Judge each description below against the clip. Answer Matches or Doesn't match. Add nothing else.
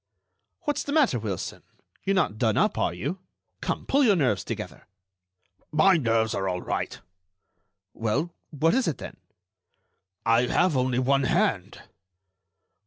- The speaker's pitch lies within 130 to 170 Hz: Matches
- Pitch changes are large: Matches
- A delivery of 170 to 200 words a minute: Doesn't match